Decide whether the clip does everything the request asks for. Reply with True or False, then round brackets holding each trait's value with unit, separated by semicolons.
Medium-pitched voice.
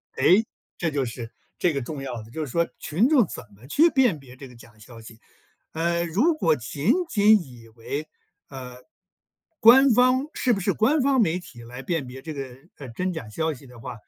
True (155 Hz)